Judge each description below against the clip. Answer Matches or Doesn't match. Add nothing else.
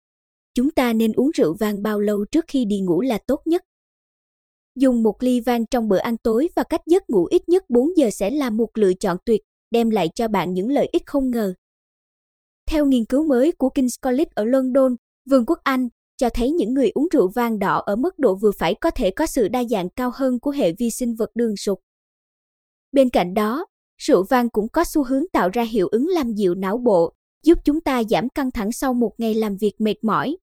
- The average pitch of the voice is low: Doesn't match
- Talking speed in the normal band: Matches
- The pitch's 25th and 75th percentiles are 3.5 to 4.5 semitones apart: Doesn't match